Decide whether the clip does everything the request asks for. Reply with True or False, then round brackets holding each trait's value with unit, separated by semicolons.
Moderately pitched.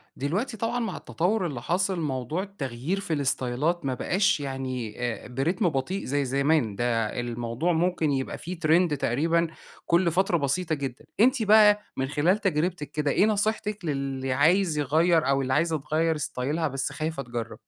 True (155 Hz)